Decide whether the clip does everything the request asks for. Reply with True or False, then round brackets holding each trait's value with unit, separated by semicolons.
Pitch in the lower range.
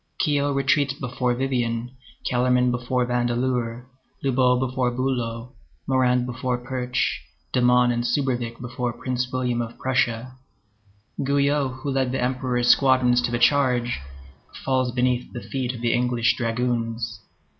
True (125 Hz)